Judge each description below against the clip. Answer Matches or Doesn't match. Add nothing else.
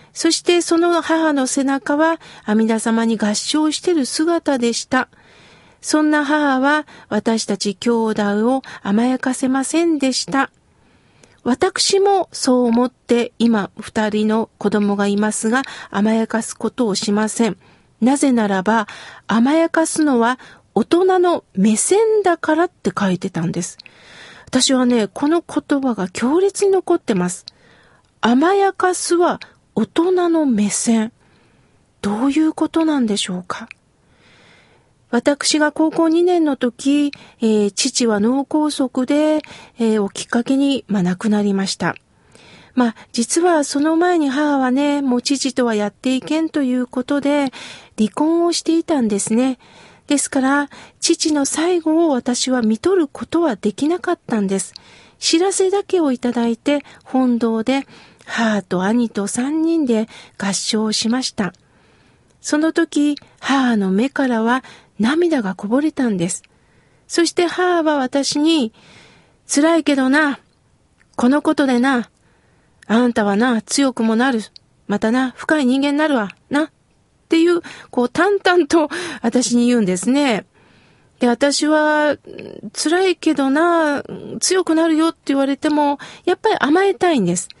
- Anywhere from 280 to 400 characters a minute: Doesn't match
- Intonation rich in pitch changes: Matches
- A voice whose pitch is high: Matches